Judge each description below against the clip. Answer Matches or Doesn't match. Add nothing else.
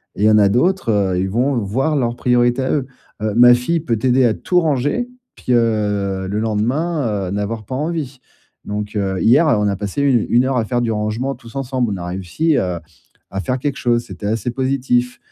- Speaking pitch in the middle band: Doesn't match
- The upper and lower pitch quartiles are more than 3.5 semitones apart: Matches